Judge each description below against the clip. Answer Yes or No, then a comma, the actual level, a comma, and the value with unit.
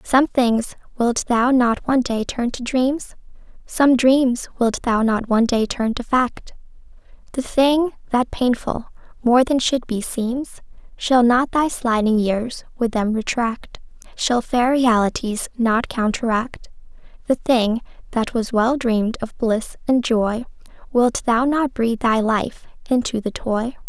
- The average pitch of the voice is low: No, high, 240 Hz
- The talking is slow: No, average, 155 wpm